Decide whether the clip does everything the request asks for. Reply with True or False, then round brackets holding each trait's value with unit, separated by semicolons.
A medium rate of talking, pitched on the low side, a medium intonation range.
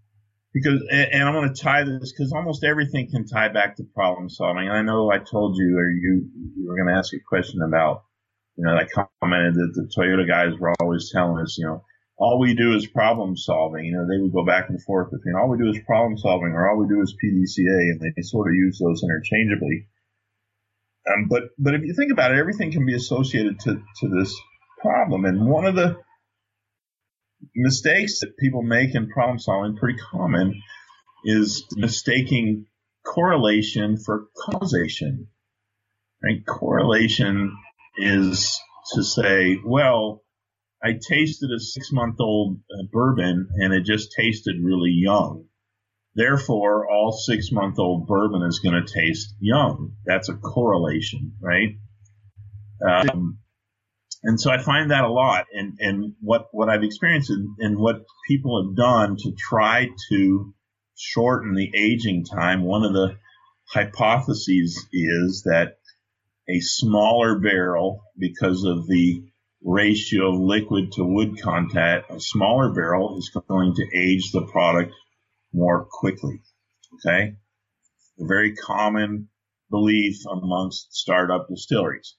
True (155 wpm; 105 Hz; 3.7 semitones)